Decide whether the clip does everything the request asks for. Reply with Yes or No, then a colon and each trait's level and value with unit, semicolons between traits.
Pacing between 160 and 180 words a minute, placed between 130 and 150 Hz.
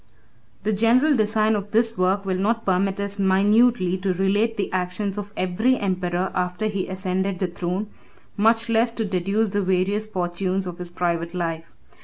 No: average, 175 wpm; high, 195 Hz